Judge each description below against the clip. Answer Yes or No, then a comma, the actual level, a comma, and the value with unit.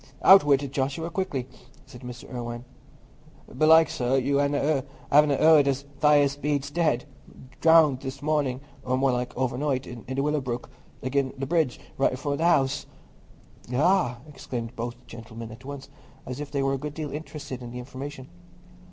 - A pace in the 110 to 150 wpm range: No, average, 170 wpm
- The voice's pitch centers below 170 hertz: Yes, low, 135 Hz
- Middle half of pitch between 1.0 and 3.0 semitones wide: Yes, narrow, 2.6 semitones